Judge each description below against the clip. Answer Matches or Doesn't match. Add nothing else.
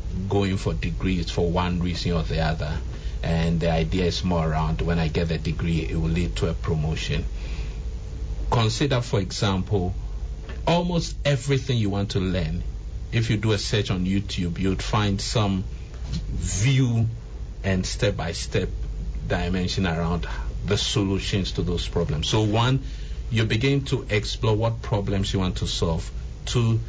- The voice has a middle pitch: Doesn't match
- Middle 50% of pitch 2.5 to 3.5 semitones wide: Doesn't match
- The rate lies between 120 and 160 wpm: Matches